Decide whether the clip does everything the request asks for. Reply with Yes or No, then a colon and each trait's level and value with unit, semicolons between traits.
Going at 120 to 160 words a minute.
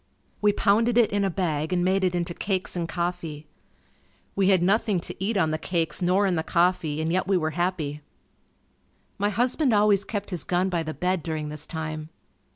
No: average, 200 wpm